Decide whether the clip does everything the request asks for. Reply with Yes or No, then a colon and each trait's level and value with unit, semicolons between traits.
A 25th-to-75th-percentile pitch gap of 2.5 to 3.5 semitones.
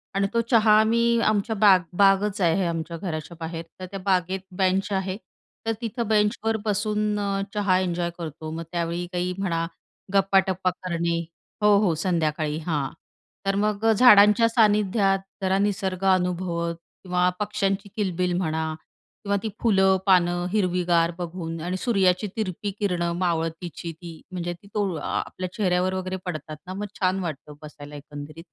Yes: average, 3.1 semitones